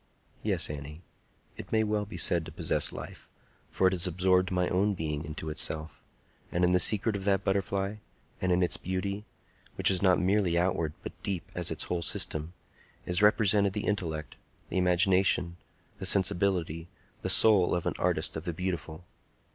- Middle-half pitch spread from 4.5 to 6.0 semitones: No, narrow, 2.5 semitones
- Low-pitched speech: Yes, very low, 90 Hz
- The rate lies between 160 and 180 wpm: Yes, average, 170 wpm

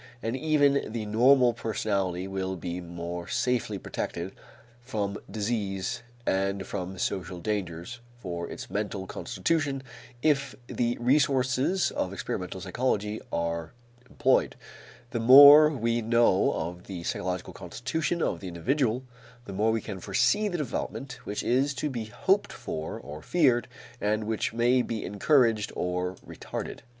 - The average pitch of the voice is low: Yes, low, 110 Hz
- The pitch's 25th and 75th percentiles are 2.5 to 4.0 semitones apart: No, wide, 5.4 semitones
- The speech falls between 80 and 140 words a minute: Yes, slow, 135 wpm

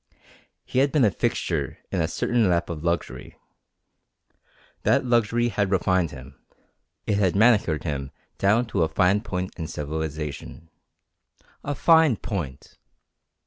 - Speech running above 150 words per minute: No, slow, 135 wpm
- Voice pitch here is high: No, very low, 95 Hz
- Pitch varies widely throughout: Yes, wide, 6.1 semitones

